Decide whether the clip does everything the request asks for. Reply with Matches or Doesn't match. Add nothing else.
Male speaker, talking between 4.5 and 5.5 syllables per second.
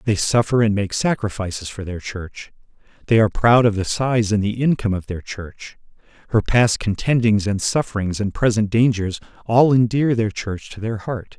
Matches